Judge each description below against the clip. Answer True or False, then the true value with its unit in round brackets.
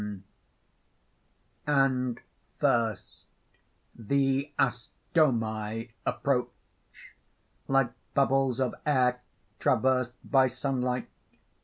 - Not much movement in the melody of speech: True (2.3 semitones)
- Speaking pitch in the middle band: False (125 Hz)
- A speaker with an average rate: False (65 wpm)